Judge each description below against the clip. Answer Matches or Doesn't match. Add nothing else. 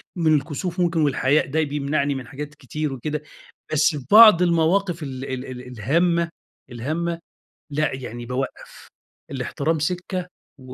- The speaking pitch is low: Doesn't match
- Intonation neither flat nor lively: Matches